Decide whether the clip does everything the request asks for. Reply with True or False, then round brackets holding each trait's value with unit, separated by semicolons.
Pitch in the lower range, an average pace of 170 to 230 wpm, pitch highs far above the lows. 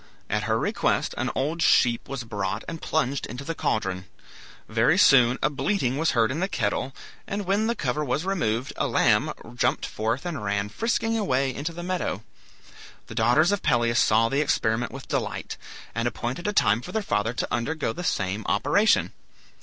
True (130 Hz; 185 wpm; 6.6 semitones)